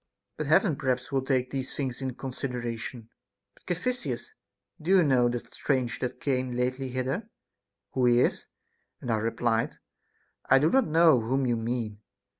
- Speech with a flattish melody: Yes, narrow, 2.2 semitones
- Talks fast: No, average, 165 wpm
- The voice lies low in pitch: Yes, low, 130 Hz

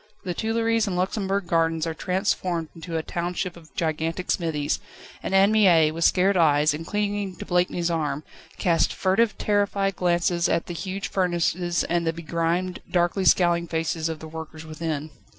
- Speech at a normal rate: Yes, average, 165 wpm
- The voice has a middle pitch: Yes, medium, 175 Hz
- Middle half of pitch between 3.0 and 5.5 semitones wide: No, narrow, 2.6 semitones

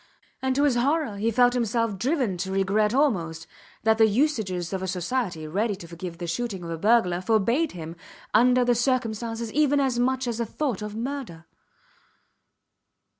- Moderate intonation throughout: Yes, average, 5.0 semitones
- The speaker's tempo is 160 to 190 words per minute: Yes, average, 175 wpm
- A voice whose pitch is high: Yes, high, 225 Hz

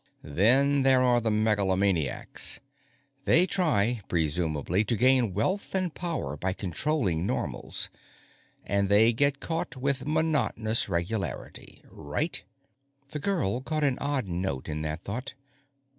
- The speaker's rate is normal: No, slow, 130 wpm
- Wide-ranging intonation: Yes, wide, 7.1 semitones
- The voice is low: Yes, low, 110 Hz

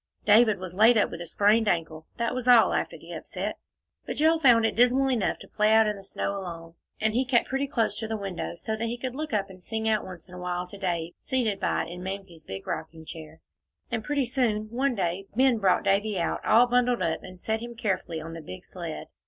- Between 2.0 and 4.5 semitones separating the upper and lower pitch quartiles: No, average, 4.9 semitones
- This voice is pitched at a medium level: No, high, 215 Hz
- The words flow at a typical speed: No, fast, 245 wpm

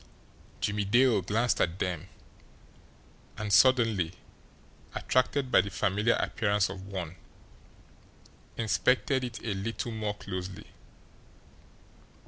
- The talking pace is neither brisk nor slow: No, slow, 100 wpm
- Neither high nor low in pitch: No, low, 105 Hz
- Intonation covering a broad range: No, average, 3.7 semitones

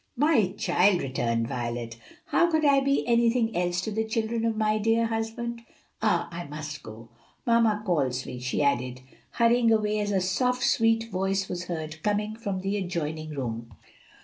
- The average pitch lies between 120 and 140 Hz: No, high, 200 Hz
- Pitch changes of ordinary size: No, wide, 6.9 semitones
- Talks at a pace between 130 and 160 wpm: No, average, 170 wpm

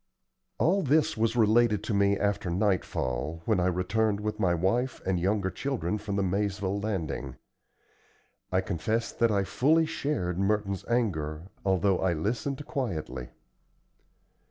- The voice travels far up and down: No, average, 3.8 semitones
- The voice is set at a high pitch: No, low, 100 Hz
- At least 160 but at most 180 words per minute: No, slow, 135 wpm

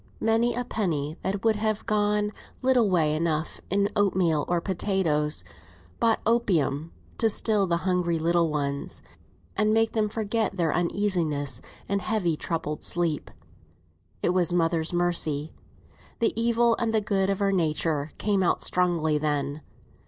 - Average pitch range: Yes, average, 4.9 semitones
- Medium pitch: Yes, medium, 180 Hz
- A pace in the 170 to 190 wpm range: No, average, 145 wpm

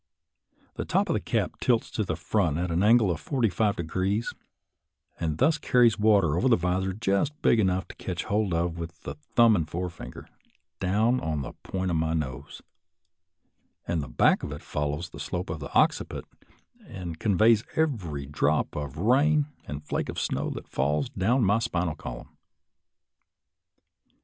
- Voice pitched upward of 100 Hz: No, very low, 90 Hz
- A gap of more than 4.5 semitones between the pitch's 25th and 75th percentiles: Yes, wide, 5.6 semitones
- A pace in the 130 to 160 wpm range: No, average, 170 wpm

